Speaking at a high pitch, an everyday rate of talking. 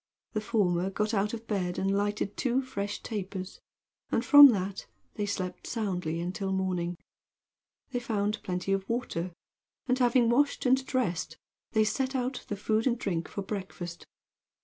Yes: high, 205 Hz; average, 155 wpm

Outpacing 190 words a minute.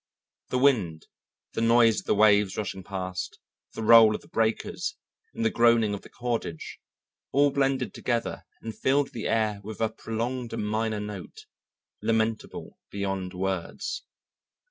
No: average, 145 wpm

